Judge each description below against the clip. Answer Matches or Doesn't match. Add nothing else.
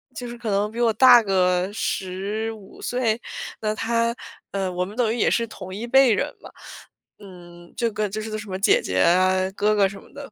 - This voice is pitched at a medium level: Doesn't match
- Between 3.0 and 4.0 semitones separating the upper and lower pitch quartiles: Matches